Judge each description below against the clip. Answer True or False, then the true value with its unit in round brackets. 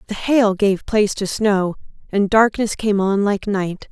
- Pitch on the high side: True (205 Hz)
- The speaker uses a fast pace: False (185 wpm)